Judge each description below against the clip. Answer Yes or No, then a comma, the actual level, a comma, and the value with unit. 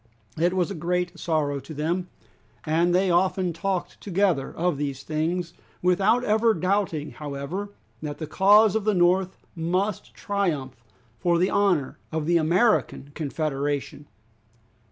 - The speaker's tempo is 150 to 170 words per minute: No, slow, 135 wpm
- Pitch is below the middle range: No, medium, 175 Hz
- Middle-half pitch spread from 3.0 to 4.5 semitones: Yes, average, 3.8 semitones